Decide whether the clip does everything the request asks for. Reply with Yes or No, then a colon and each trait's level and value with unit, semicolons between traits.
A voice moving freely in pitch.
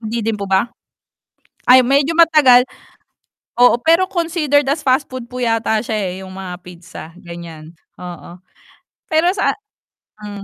Yes: wide, 7.1 semitones